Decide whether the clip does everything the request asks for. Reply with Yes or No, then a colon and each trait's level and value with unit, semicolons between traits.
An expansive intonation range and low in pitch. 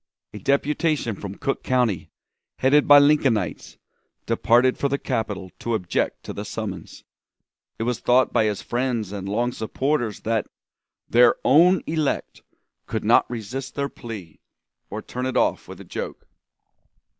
No: average, 4.3 semitones; low, 120 Hz